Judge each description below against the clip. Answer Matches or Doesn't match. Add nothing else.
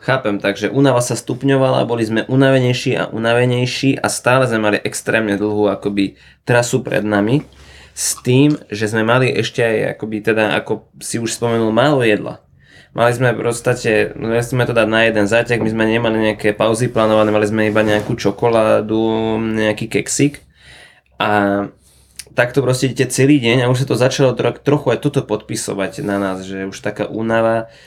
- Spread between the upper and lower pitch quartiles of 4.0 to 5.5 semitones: Doesn't match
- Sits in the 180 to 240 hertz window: Doesn't match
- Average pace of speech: Doesn't match